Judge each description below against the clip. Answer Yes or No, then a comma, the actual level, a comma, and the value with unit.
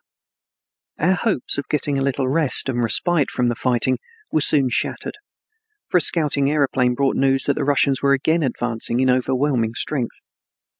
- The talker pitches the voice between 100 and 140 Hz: Yes, low, 135 Hz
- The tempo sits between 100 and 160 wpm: No, average, 170 wpm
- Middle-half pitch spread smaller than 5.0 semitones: Yes, average, 2.7 semitones